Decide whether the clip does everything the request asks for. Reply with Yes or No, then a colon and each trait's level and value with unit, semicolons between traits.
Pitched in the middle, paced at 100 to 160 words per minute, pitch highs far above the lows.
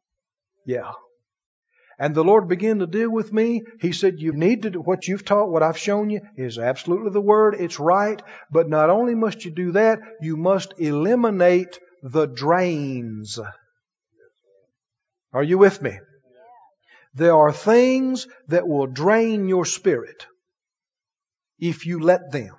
Yes: medium, 180 Hz; average, 150 wpm; wide, 5.8 semitones